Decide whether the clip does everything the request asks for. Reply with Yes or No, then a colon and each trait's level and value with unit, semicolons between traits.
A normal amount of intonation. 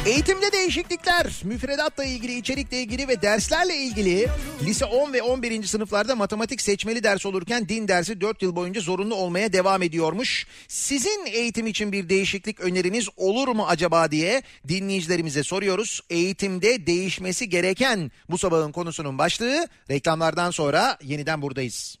No: wide, 5.7 semitones